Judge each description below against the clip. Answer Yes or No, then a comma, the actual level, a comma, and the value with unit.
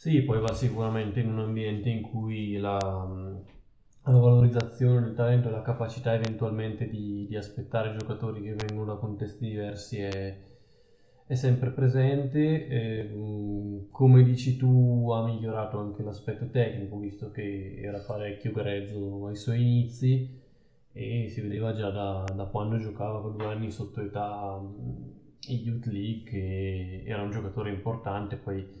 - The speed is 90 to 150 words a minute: Yes, average, 145 wpm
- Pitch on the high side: No, low, 110 Hz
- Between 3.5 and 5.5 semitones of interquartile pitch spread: No, average, 2.8 semitones